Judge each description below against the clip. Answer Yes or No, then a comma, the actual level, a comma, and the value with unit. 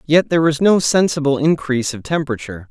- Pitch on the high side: No, medium, 145 Hz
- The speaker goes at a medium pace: Yes, average, 175 wpm